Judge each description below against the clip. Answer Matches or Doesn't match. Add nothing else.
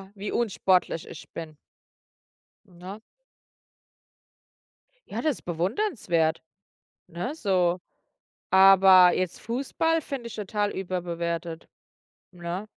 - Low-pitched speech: Doesn't match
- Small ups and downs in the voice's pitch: Doesn't match